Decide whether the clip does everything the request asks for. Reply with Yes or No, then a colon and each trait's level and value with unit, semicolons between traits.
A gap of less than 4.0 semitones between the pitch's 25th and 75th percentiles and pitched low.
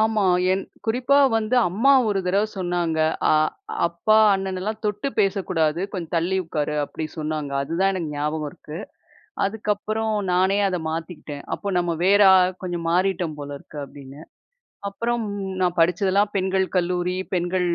No: average, 3.6 semitones; medium, 185 Hz